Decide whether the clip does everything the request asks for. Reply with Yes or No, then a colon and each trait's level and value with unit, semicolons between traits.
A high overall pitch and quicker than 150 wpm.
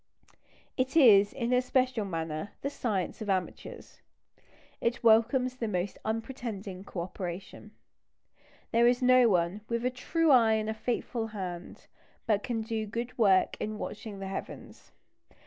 No: high, 220 Hz; average, 145 wpm